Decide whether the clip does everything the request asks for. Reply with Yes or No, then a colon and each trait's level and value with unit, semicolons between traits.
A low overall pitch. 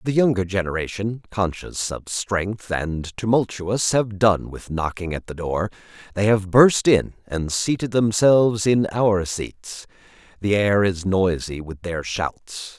Yes: low, 100 Hz